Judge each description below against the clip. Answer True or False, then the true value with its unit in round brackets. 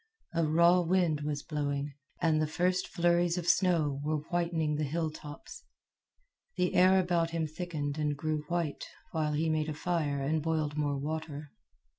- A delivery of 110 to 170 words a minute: True (160 wpm)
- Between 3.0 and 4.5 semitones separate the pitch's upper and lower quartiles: False (2.5 semitones)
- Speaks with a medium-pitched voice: True (155 Hz)